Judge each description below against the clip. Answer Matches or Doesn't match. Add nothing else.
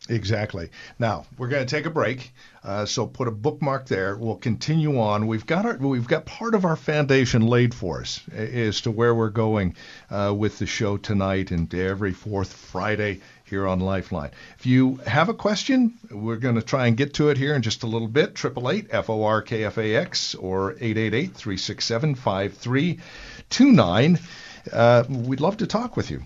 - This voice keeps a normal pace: Matches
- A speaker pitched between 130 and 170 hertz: Doesn't match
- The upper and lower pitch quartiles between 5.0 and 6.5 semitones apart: Matches